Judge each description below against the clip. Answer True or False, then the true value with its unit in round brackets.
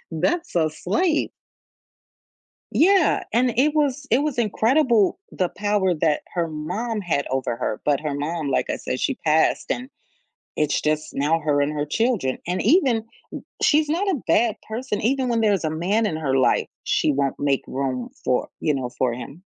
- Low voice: False (180 Hz)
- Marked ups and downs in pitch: True (8.7 semitones)